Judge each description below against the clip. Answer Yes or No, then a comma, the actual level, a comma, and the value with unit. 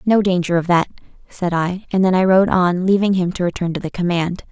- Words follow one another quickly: Yes, fast, 240 wpm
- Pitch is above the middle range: No, medium, 180 Hz